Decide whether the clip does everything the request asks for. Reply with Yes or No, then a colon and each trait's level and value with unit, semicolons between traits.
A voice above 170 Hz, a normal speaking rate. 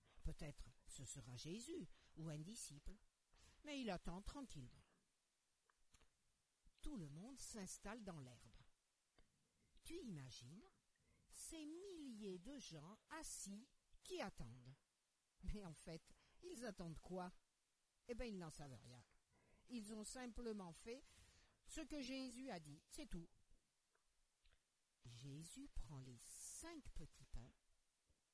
No: medium, 185 Hz; slow, 115 wpm